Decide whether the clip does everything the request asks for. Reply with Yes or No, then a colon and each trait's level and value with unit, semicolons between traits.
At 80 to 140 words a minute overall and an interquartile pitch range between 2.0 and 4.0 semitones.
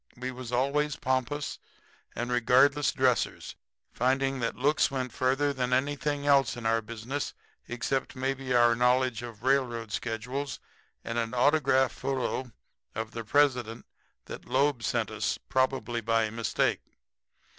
Yes: slow, 135 wpm; narrow, 2.5 semitones